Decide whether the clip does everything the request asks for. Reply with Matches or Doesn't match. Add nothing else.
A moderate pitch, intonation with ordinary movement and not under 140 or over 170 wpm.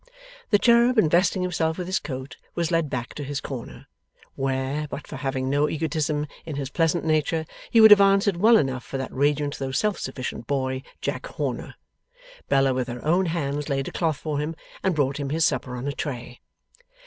Doesn't match